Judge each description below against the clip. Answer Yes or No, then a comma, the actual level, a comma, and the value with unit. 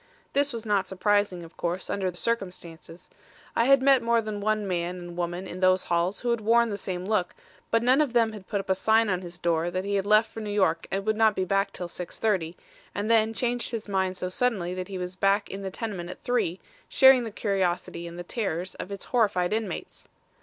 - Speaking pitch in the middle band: No, high, 195 Hz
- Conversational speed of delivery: No, fast, 230 wpm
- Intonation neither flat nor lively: Yes, average, 3.7 semitones